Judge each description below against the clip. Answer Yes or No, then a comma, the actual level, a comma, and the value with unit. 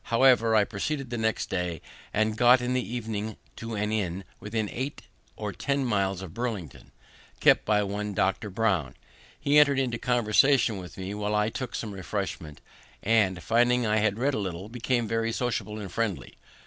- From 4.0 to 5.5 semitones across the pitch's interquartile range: No, average, 3.3 semitones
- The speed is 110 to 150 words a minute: No, average, 175 wpm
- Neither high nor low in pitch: No, low, 110 Hz